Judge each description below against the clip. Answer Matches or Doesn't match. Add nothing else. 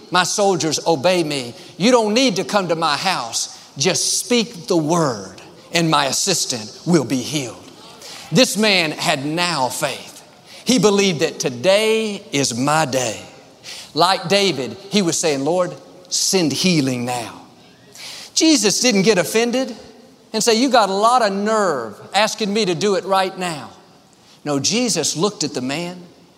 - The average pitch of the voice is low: Doesn't match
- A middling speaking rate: Matches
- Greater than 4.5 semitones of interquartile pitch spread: Matches